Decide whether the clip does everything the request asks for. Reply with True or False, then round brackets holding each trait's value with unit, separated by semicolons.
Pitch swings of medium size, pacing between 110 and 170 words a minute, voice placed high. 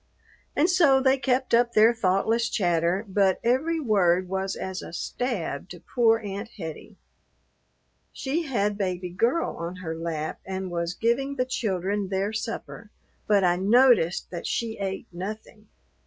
True (4.7 semitones; 150 wpm; 205 Hz)